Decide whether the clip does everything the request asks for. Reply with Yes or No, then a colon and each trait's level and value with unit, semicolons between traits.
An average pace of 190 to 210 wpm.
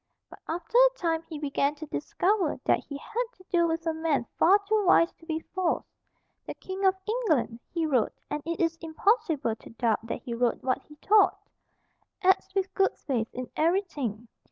Yes: average, 195 wpm